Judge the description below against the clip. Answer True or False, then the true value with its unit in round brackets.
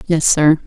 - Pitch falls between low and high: True (155 Hz)